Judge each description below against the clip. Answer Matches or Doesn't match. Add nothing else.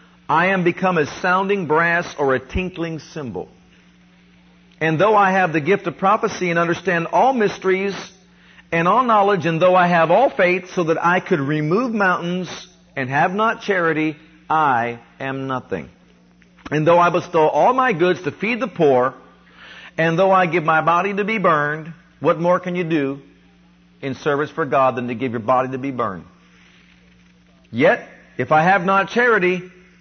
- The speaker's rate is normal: Matches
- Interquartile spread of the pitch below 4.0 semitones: Doesn't match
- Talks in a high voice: Doesn't match